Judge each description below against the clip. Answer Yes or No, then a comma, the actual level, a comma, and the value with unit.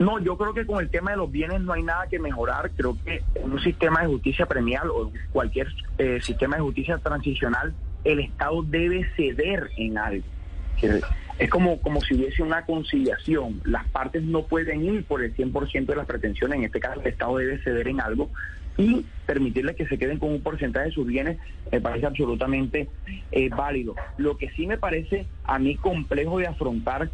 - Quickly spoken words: Yes, fast, 195 wpm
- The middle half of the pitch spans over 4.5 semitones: Yes, average, 5.2 semitones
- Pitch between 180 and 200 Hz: No, medium, 140 Hz